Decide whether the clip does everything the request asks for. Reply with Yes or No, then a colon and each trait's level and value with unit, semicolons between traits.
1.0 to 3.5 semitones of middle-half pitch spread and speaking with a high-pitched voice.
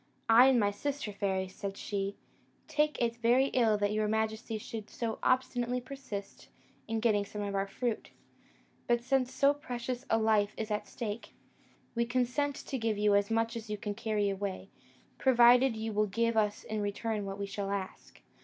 Yes: average, 3.0 semitones; high, 220 Hz